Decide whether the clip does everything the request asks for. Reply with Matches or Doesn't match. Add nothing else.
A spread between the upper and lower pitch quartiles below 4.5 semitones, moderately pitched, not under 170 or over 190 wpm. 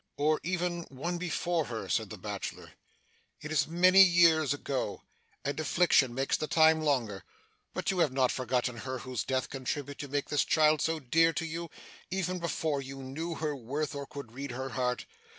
Matches